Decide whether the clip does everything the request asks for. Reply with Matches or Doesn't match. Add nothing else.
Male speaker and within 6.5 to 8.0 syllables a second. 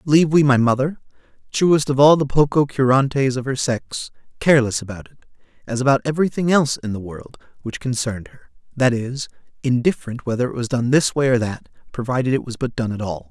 Matches